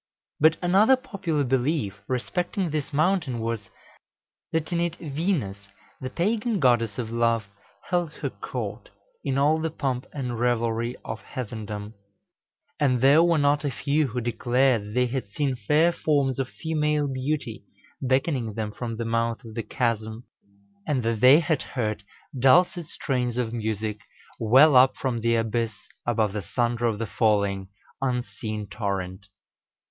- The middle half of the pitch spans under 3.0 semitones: No, average, 4.9 semitones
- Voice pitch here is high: No, low, 125 Hz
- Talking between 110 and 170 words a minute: Yes, average, 150 wpm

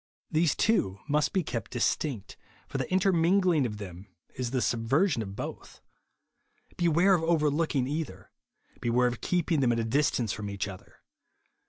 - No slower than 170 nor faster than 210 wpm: No, average, 160 wpm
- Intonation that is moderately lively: No, wide, 6.6 semitones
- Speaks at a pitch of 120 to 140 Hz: Yes, low, 135 Hz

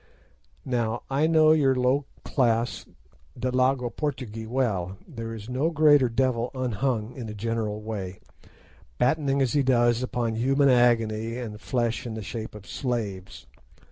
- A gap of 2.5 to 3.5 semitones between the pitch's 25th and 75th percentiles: Yes, average, 3.0 semitones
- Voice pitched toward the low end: Yes, low, 120 Hz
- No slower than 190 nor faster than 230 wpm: No, average, 140 wpm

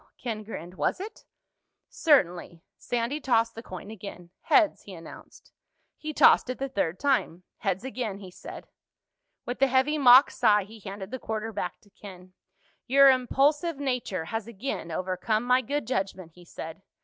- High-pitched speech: Yes, high, 225 Hz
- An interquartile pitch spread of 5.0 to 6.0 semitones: Yes, wide, 5.6 semitones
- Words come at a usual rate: Yes, average, 160 wpm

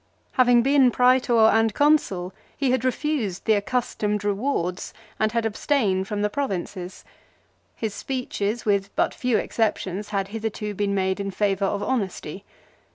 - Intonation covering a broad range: No, average, 4.0 semitones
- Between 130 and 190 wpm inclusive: Yes, average, 150 wpm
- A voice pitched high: Yes, high, 210 Hz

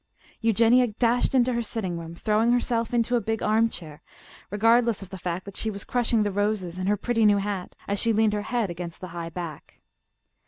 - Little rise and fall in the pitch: No, average, 3.7 semitones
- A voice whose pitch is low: No, high, 210 Hz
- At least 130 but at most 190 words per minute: No, fast, 205 wpm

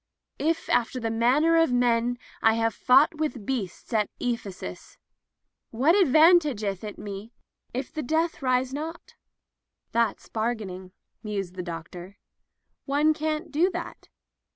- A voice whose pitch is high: Yes, high, 245 Hz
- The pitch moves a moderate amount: No, wide, 6.4 semitones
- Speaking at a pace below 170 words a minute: Yes, slow, 135 wpm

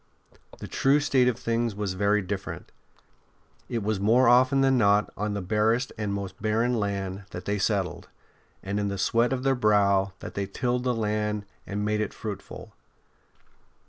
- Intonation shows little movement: No, average, 3.1 semitones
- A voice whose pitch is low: Yes, low, 105 Hz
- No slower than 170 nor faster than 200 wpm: Yes, average, 175 wpm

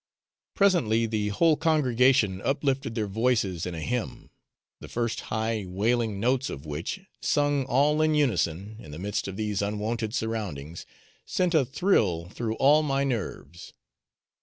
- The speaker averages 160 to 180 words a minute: No, average, 145 wpm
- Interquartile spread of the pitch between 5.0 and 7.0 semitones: Yes, wide, 5.4 semitones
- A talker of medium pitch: No, low, 115 Hz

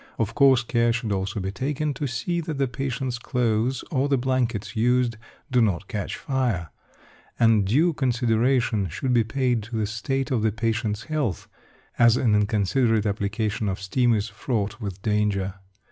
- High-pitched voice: No, low, 115 Hz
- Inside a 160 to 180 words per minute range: Yes, average, 165 wpm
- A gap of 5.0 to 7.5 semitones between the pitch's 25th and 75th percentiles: No, average, 3.6 semitones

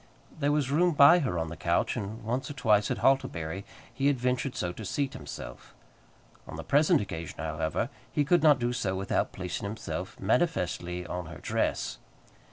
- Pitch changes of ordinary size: No, wide, 7.9 semitones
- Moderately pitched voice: No, low, 110 Hz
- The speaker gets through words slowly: No, average, 180 wpm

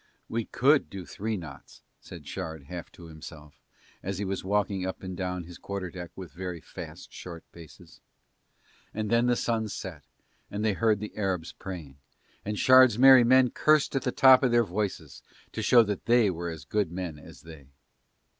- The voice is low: Yes, very low, 95 Hz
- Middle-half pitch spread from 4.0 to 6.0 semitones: Yes, average, 4.9 semitones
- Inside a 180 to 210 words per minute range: Yes, average, 185 wpm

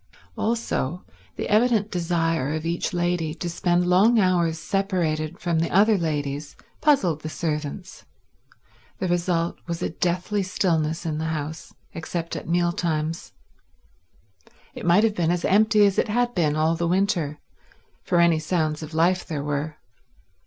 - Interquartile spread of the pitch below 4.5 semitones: Yes, average, 2.8 semitones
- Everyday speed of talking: Yes, average, 150 wpm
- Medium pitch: Yes, medium, 170 Hz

